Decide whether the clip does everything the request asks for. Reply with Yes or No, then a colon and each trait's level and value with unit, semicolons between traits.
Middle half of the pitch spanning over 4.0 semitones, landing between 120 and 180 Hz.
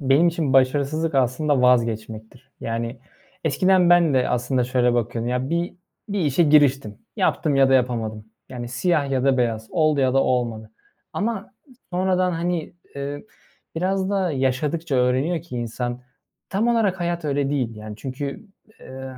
Yes: average, 5.2 semitones; low, 135 Hz